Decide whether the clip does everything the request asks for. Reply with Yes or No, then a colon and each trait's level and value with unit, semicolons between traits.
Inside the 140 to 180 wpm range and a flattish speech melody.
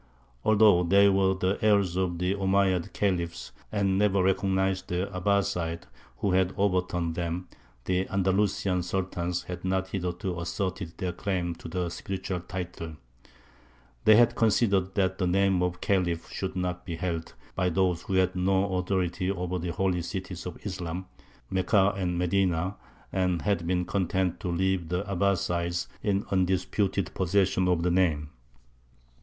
Yes: average, 150 wpm; narrow, 1.6 semitones